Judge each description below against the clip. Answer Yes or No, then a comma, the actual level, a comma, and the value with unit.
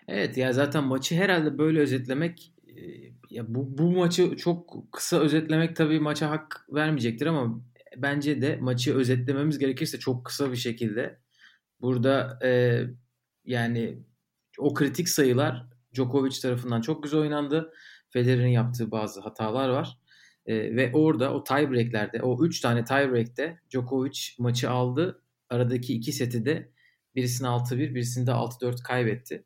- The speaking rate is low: No, average, 135 wpm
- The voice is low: Yes, low, 130 Hz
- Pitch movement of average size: Yes, average, 3.5 semitones